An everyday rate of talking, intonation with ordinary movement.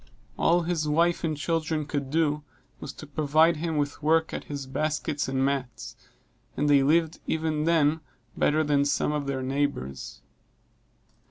No: average, 160 wpm; narrow, 2.2 semitones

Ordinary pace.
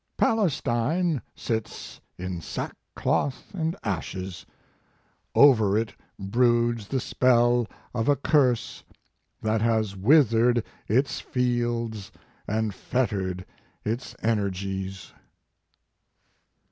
No: slow, 85 wpm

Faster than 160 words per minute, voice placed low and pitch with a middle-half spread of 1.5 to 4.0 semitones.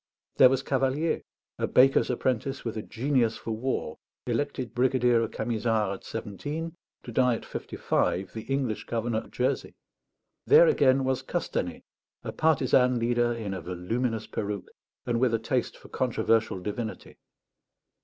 No: average, 150 wpm; low, 120 Hz; average, 2.9 semitones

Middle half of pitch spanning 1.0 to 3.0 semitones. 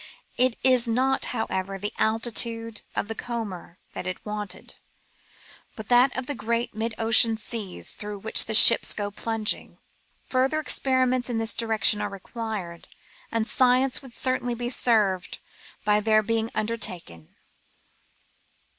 Yes: narrow, 2.6 semitones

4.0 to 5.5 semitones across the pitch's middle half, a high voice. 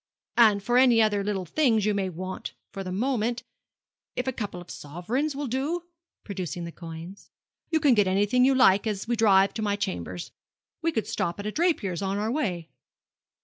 Yes: average, 4.9 semitones; high, 205 Hz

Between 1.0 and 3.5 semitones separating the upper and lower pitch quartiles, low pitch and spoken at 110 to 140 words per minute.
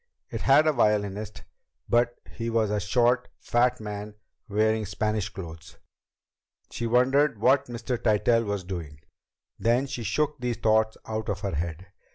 No: average, 2.9 semitones; low, 110 Hz; average, 150 wpm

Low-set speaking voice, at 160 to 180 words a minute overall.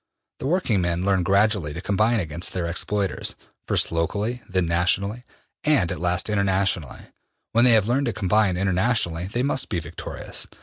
Yes: low, 100 Hz; average, 165 wpm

